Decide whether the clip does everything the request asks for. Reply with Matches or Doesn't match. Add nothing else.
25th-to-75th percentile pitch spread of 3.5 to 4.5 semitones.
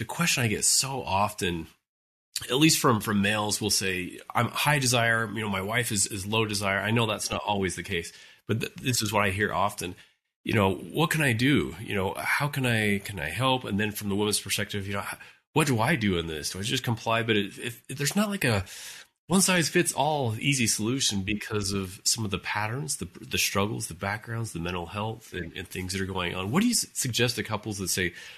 Matches